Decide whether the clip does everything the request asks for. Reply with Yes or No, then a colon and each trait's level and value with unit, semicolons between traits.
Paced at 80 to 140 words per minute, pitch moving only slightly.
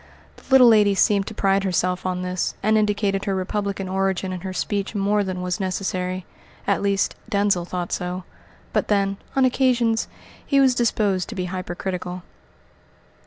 No: average, 165 wpm; narrow, 2.1 semitones